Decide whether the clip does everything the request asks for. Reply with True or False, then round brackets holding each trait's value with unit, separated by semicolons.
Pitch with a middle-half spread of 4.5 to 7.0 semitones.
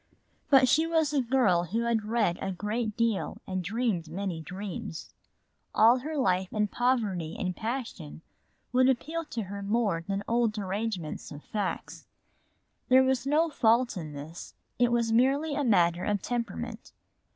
True (5.2 semitones)